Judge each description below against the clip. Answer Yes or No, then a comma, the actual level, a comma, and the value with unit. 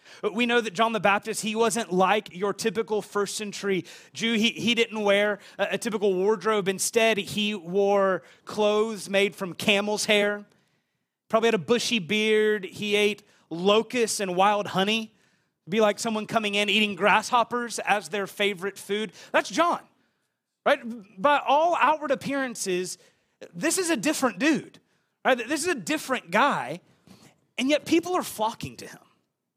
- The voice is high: Yes, high, 215 Hz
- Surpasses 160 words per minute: No, average, 155 wpm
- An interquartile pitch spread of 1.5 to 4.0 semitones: Yes, narrow, 2.5 semitones